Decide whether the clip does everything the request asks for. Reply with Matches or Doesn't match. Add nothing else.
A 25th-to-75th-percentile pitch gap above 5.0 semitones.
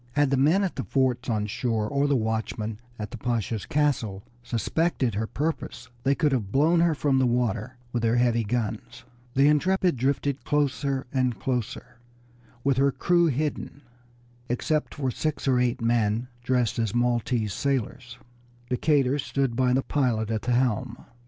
Doesn't match